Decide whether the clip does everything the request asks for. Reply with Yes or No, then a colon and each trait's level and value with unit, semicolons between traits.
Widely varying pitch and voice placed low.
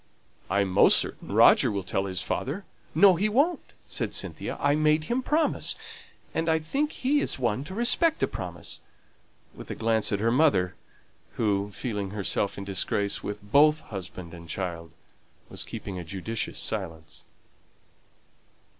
Yes: wide, 8.7 semitones; low, 105 Hz